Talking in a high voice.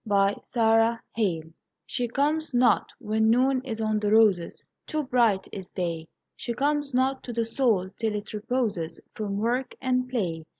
Yes: high, 225 Hz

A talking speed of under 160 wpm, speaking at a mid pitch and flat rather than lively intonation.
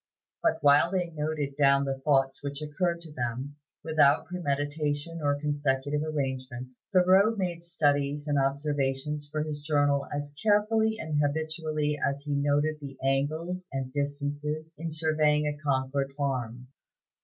Yes: average, 140 wpm; medium, 145 Hz; narrow, 2.1 semitones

